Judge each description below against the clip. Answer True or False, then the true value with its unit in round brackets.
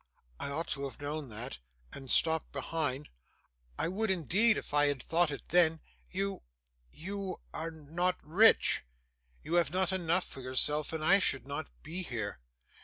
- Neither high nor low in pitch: True (160 Hz)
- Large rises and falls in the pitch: False (4.3 semitones)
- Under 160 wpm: False (165 wpm)